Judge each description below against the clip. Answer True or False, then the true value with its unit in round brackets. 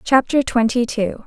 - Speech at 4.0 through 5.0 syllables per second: True (4.3 syllables/s)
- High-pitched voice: True (240 Hz)